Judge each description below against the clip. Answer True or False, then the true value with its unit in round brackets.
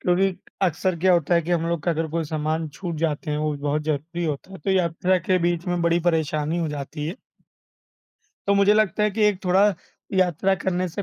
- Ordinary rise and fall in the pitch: True (3.0 semitones)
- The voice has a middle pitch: True (170 Hz)